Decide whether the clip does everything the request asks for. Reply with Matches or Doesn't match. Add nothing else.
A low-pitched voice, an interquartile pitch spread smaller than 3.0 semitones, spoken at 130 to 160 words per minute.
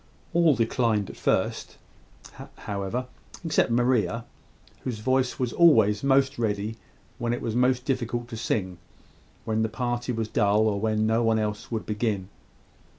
Matches